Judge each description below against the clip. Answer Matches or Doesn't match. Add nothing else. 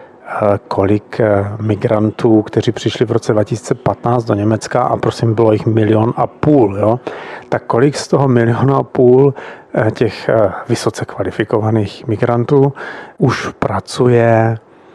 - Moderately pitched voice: Doesn't match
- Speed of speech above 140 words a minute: Doesn't match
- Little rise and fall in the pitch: Matches